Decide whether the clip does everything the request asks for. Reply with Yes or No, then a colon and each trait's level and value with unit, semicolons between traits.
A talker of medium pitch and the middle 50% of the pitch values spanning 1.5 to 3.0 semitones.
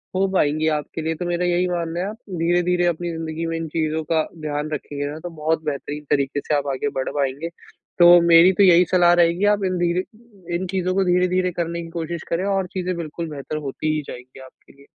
Yes: medium, 170 Hz; narrow, 2.5 semitones